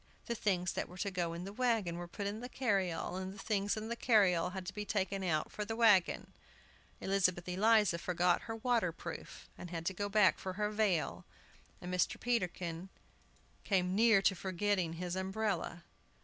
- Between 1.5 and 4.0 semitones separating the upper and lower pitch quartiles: Yes, average, 2.9 semitones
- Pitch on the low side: No, high, 190 Hz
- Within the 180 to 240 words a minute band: Yes, average, 190 wpm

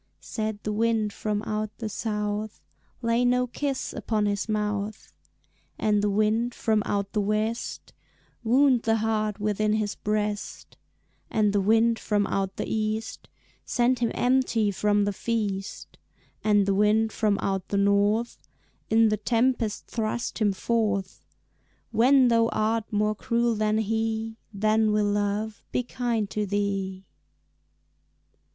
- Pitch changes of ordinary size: No, narrow, 1.6 semitones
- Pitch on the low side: No, high, 215 Hz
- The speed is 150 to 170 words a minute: No, average, 140 wpm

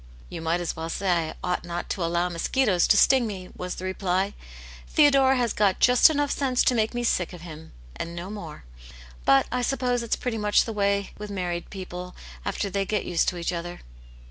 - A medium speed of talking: No, fast, 215 wpm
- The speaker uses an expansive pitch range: No, average, 5.0 semitones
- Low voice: No, high, 190 Hz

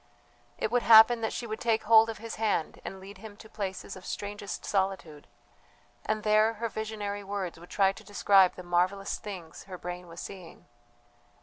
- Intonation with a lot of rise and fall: No, average, 2.7 semitones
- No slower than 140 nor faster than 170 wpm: No, average, 185 wpm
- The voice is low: No, high, 205 Hz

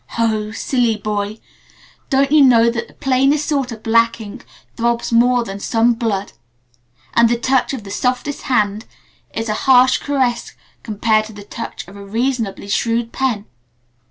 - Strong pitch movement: No, average, 2.9 semitones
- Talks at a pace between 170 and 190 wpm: No, average, 160 wpm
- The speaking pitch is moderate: No, high, 230 Hz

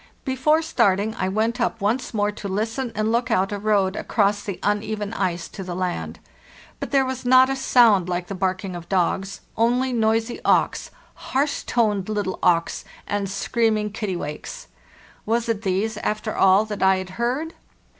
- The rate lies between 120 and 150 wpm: No, average, 170 wpm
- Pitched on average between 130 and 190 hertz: No, high, 210 Hz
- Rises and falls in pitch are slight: No, average, 3.5 semitones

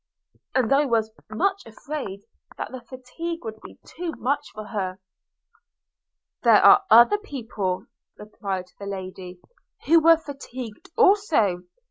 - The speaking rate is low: Yes, slow, 120 wpm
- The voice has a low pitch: No, high, 235 Hz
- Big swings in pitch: Yes, wide, 7.8 semitones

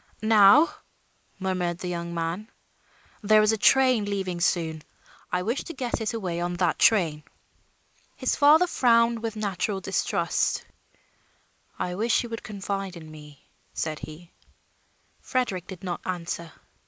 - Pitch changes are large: No, average, 4.7 semitones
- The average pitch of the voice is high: Yes, high, 195 Hz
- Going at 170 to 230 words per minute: No, average, 140 wpm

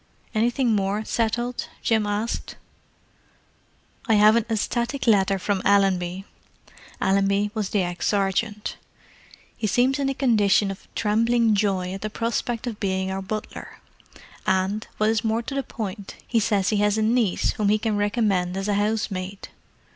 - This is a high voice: Yes, high, 210 Hz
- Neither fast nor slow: Yes, average, 155 wpm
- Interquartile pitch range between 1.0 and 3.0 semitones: Yes, narrow, 2.6 semitones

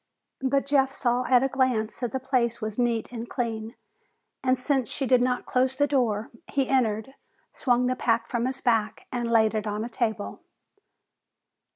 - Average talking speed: Yes, average, 180 wpm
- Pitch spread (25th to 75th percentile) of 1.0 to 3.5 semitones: Yes, narrow, 2.5 semitones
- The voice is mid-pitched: No, high, 245 Hz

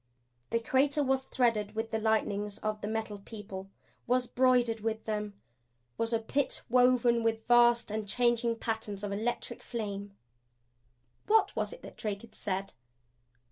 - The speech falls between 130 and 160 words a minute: Yes, average, 150 wpm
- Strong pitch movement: No, narrow, 2.5 semitones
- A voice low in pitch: No, high, 225 Hz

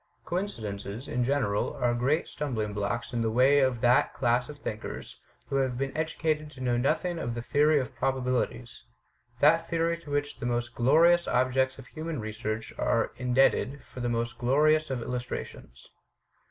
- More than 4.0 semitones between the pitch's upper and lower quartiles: No, average, 3.7 semitones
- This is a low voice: Yes, low, 130 Hz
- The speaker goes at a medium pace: Yes, average, 170 wpm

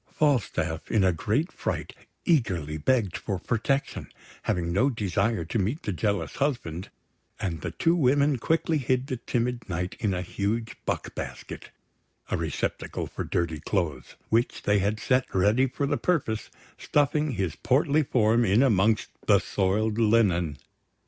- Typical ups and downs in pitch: No, wide, 5.9 semitones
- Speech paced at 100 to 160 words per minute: Yes, average, 150 wpm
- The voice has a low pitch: Yes, low, 110 Hz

